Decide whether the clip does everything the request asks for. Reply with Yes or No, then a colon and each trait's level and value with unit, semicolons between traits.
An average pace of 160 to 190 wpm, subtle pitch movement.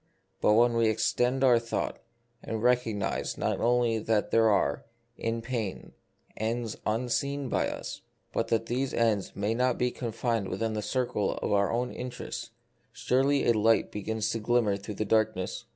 Yes: average, 170 wpm; narrow, 2.1 semitones